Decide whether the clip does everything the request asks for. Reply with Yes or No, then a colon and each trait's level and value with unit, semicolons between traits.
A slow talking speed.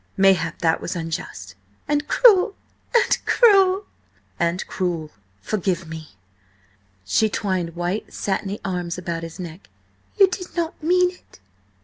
Yes: slow, 125 wpm